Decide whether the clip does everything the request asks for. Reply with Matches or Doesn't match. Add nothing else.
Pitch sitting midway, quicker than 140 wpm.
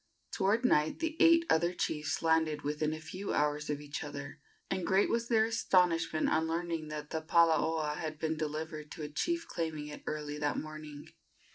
Matches